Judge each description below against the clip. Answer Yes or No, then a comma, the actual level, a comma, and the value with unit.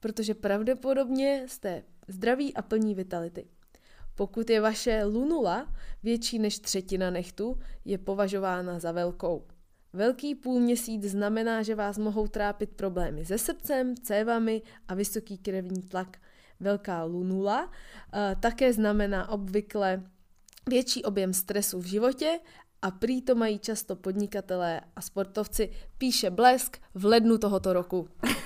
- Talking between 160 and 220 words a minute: No, average, 125 wpm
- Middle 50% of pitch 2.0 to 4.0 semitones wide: Yes, average, 3.3 semitones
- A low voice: No, high, 205 Hz